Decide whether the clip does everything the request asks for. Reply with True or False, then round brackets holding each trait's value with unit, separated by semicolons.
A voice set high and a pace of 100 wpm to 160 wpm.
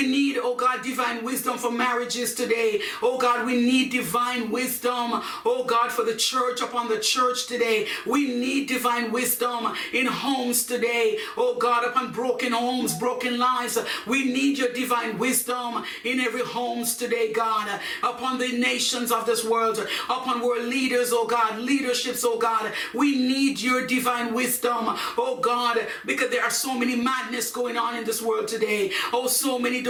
False (245 Hz; 170 wpm)